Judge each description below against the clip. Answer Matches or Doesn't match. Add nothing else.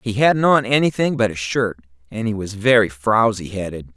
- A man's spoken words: Matches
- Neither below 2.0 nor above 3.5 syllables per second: Doesn't match